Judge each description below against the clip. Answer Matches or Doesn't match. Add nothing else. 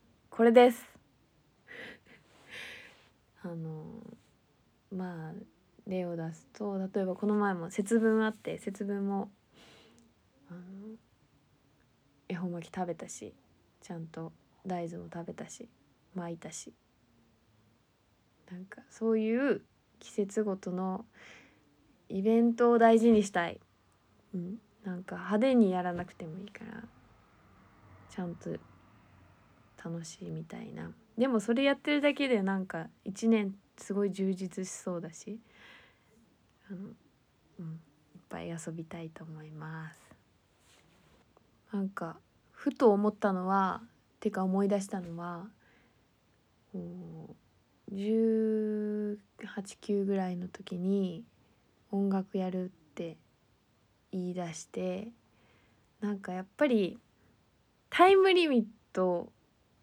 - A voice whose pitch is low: Doesn't match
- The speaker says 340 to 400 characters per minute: Doesn't match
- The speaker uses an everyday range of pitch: Matches